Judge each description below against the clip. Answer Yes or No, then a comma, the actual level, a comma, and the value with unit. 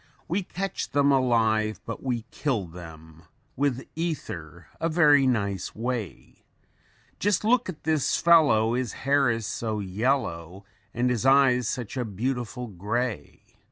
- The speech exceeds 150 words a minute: No, slow, 135 wpm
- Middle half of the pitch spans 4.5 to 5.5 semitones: Yes, average, 4.9 semitones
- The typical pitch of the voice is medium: No, low, 125 Hz